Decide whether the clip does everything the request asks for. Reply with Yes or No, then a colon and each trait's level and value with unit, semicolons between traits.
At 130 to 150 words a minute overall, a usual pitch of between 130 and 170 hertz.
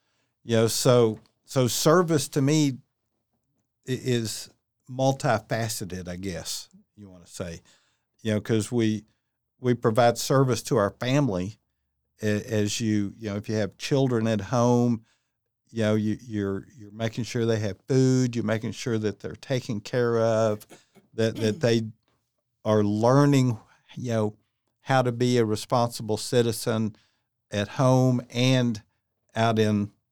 No: average, 140 wpm; low, 115 Hz